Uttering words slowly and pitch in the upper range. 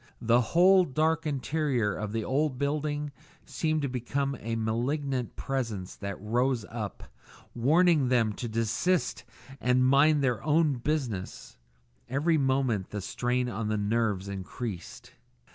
No: slow, 130 wpm; low, 125 Hz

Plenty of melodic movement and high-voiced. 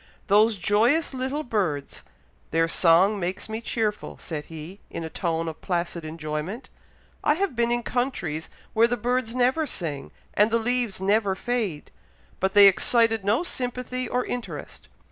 Yes: wide, 6.1 semitones; high, 215 Hz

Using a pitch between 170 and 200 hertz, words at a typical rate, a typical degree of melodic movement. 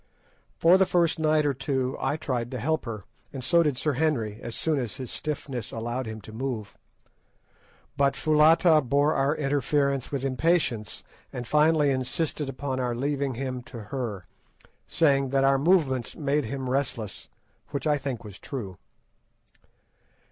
No: low, 135 Hz; average, 155 wpm; average, 3.5 semitones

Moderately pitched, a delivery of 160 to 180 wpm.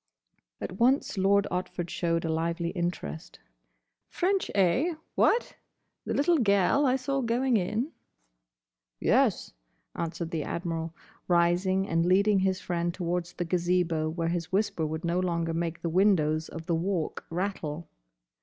No: medium, 175 Hz; slow, 135 wpm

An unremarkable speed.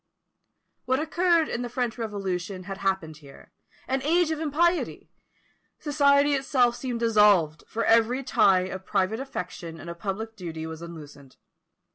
Yes: average, 145 wpm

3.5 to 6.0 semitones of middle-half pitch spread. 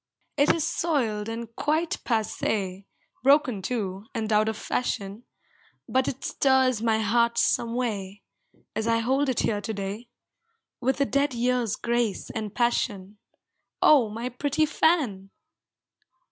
Yes: average, 3.8 semitones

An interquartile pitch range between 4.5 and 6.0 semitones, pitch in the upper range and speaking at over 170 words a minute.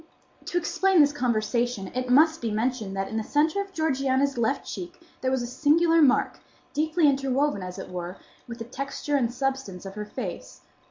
Yes: average, 5.1 semitones; very high, 260 Hz; average, 185 wpm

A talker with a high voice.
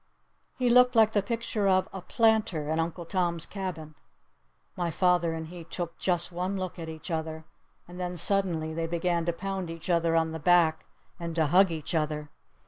No: medium, 170 Hz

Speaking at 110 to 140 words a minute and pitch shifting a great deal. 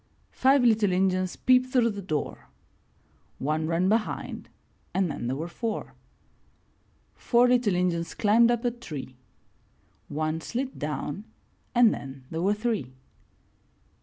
Yes: slow, 135 wpm; wide, 6.9 semitones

